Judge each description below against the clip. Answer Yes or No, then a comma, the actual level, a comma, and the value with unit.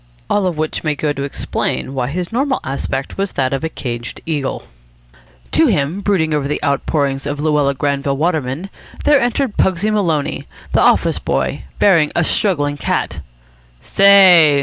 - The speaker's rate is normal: Yes, average, 160 wpm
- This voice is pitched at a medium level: Yes, medium, 150 Hz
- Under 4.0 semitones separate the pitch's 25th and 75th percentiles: No, average, 5.1 semitones